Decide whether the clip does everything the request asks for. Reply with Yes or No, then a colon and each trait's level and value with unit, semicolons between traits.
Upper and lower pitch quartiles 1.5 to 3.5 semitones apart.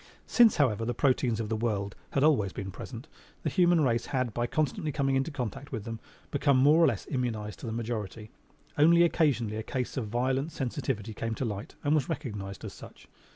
No: average, 4.5 semitones